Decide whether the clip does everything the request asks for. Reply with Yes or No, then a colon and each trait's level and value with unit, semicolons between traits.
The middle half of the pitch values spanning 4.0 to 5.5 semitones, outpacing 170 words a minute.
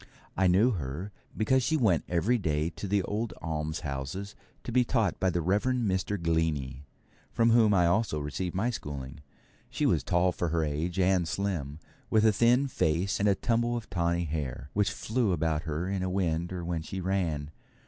Yes: average, 4.5 semitones; average, 190 wpm